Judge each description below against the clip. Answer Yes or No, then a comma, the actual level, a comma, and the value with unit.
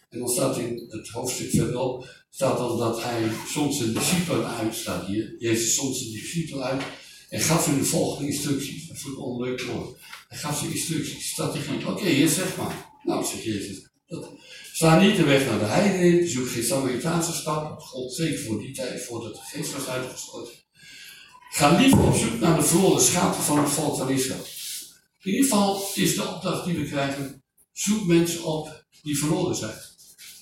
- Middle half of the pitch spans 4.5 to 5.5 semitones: Yes, average, 4.9 semitones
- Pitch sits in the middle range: Yes, medium, 145 Hz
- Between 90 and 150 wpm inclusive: No, average, 185 wpm